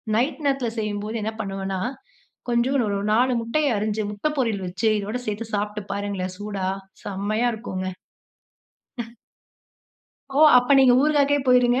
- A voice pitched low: No, high, 215 Hz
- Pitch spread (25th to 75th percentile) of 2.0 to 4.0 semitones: Yes, average, 3.5 semitones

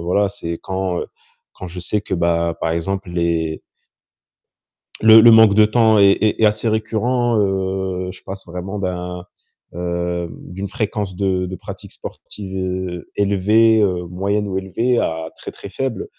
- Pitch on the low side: Yes, very low, 95 Hz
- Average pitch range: Yes, average, 3.0 semitones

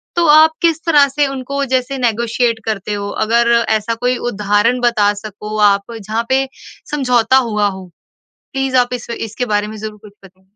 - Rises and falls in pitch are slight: No, average, 3.8 semitones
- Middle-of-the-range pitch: No, high, 230 Hz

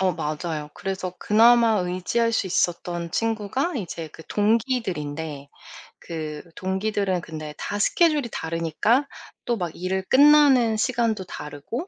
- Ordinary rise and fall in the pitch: No, wide, 5.7 semitones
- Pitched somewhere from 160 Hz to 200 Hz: Yes, high, 190 Hz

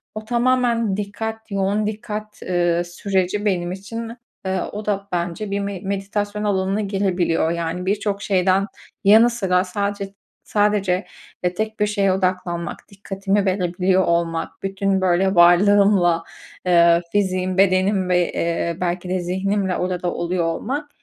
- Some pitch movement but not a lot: No, narrow, 2.3 semitones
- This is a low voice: No, high, 195 Hz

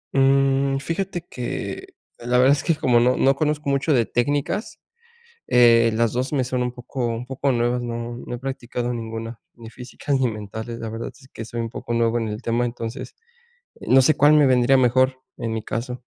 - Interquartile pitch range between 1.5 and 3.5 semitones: Yes, narrow, 2.4 semitones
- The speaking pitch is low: Yes, low, 125 Hz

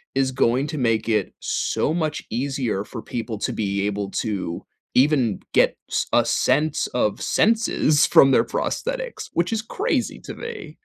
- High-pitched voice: No, low, 130 Hz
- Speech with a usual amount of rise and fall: No, wide, 6.5 semitones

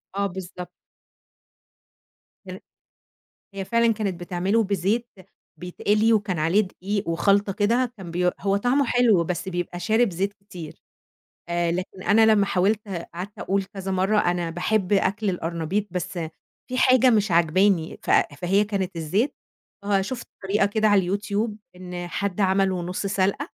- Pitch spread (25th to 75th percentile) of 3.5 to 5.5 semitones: No, average, 2.8 semitones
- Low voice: No, high, 195 Hz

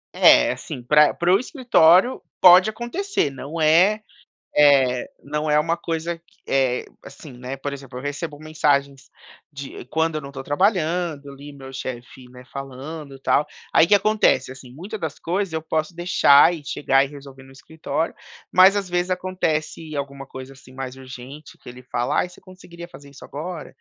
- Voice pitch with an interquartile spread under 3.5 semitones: No, average, 4.2 semitones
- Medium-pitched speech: Yes, medium, 150 Hz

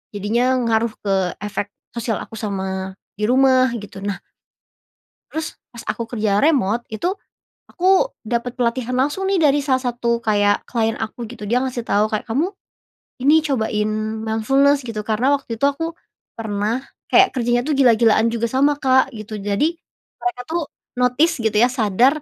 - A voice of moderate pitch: No, high, 235 Hz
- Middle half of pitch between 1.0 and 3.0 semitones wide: No, average, 3.7 semitones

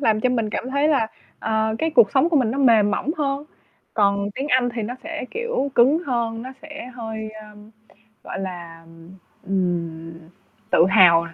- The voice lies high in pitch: Yes, high, 230 Hz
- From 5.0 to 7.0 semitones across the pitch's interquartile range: Yes, wide, 5.4 semitones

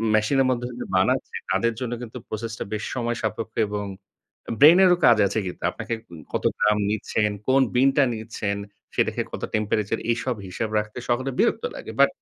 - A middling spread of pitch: Yes, average, 3.1 semitones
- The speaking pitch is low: Yes, low, 115 Hz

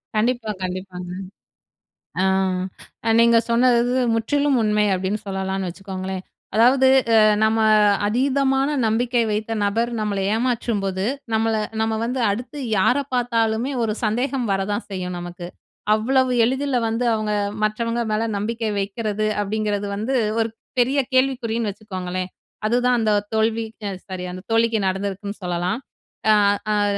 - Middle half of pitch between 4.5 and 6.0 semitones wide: No, average, 3.3 semitones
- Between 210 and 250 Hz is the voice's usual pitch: Yes, high, 220 Hz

